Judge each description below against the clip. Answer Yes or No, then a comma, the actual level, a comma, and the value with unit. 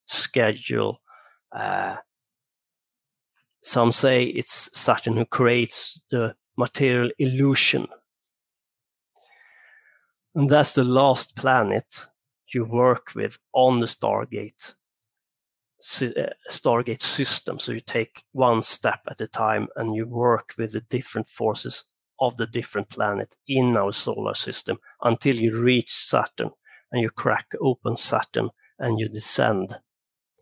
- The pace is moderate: No, slow, 115 wpm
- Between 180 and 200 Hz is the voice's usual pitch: No, low, 120 Hz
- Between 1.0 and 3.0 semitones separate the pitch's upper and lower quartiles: Yes, narrow, 2.6 semitones